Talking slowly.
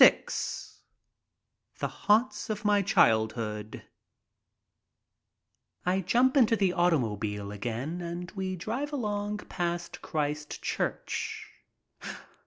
Yes: slow, 95 wpm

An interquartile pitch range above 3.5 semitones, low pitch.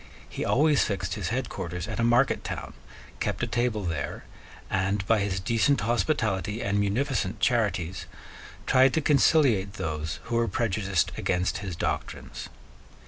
Yes: average, 4.3 semitones; low, 105 Hz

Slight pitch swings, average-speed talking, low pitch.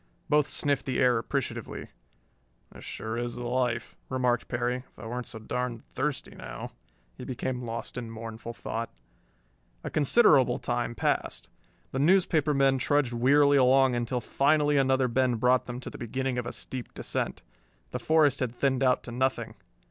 Yes: narrow, 2.2 semitones; average, 165 wpm; low, 125 Hz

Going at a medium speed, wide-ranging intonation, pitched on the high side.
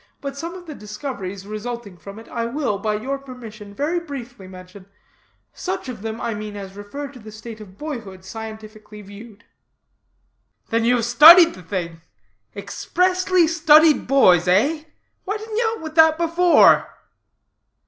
Yes: average, 160 wpm; wide, 7.0 semitones; high, 235 Hz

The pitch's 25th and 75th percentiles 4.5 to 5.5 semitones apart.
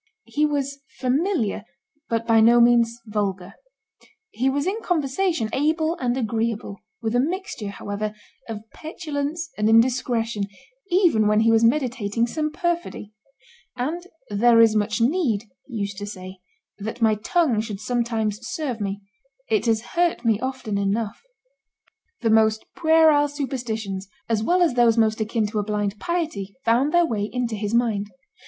Yes: average, 5.1 semitones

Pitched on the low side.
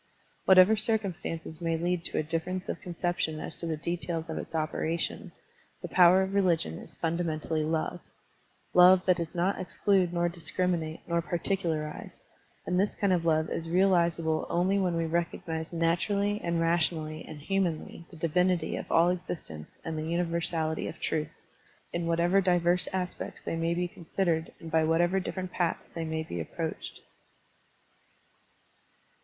No: medium, 170 Hz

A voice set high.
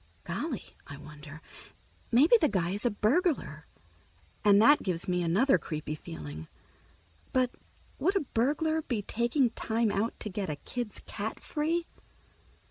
Yes: high, 215 Hz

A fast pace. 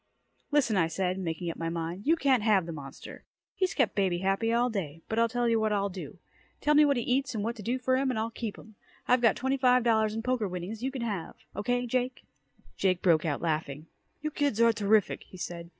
Yes: fast, 240 wpm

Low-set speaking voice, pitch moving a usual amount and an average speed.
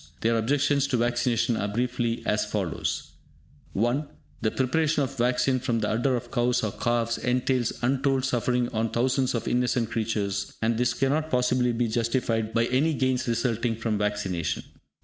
No: low, 120 Hz; narrow, 2.2 semitones; average, 165 wpm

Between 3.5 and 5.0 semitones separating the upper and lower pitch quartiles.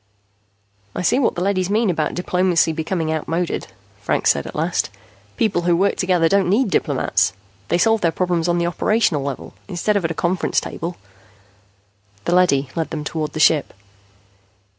No: average, 2.7 semitones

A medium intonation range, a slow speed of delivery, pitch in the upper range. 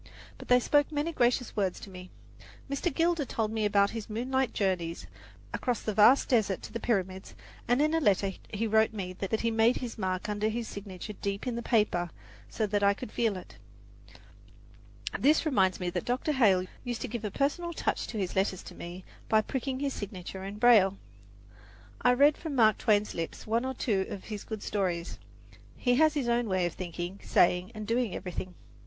No: average, 4.4 semitones; average, 195 wpm; high, 215 Hz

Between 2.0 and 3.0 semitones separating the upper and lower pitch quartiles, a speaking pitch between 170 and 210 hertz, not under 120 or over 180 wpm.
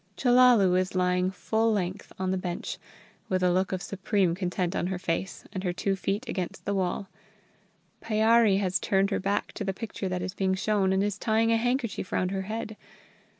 No: narrow, 2.5 semitones; high, 190 Hz; average, 195 wpm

